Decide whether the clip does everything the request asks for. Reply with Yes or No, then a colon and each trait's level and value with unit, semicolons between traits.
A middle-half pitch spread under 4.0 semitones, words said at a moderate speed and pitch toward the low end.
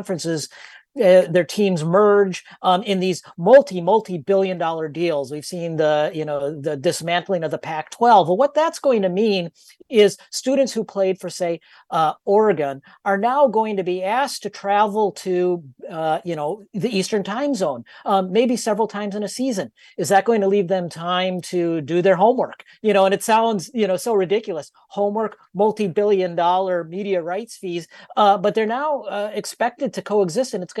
No: average, 3.2 semitones; average, 185 wpm; high, 195 Hz